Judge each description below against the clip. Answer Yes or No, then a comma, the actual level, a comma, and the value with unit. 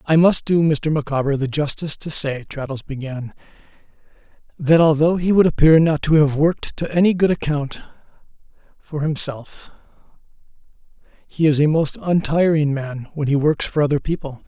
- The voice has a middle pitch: Yes, medium, 150 Hz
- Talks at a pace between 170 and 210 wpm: No, average, 160 wpm